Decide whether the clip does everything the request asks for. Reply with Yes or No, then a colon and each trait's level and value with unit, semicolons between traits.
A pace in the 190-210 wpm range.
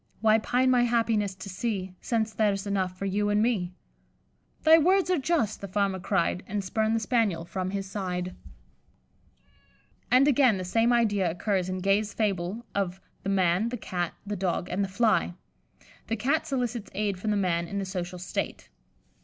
No: average, 180 wpm